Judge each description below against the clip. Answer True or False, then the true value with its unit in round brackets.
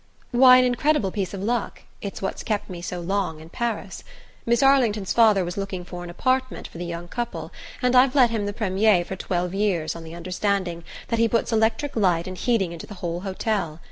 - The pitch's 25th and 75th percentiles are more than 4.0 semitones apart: True (4.6 semitones)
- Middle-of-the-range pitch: False (200 Hz)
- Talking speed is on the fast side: True (215 wpm)